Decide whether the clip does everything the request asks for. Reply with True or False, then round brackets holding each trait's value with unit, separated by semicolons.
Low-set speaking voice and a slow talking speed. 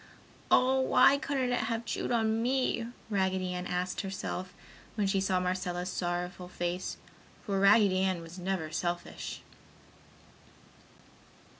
False (190 Hz; 125 wpm)